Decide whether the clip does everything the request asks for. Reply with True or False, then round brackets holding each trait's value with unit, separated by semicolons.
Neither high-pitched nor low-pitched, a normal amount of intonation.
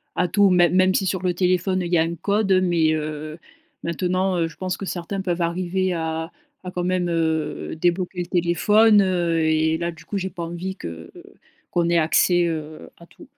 False (175 Hz; 2.2 semitones)